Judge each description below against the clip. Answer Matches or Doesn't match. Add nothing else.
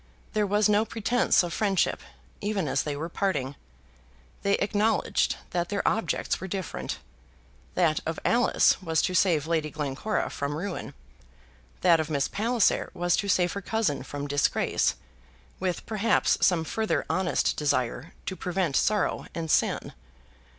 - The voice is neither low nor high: Matches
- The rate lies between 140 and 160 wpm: Matches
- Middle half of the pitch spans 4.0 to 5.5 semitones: Matches